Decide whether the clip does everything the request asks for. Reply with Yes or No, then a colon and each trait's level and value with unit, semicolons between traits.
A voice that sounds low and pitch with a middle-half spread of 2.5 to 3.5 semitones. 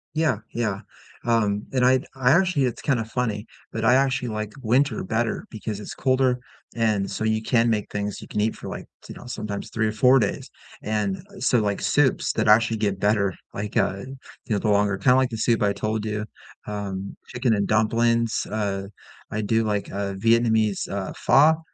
Yes: low, 110 Hz; average, 2.9 semitones